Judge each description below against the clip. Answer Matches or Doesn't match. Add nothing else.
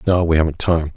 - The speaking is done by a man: Matches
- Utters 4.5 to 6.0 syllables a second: Doesn't match